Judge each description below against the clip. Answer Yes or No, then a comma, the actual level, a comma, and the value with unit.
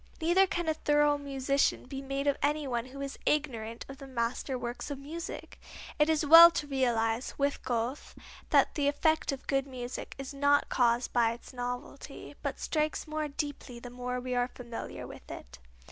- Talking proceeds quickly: No, average, 185 wpm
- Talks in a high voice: Yes, very high, 275 Hz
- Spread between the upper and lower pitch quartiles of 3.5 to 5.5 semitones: No, average, 3.1 semitones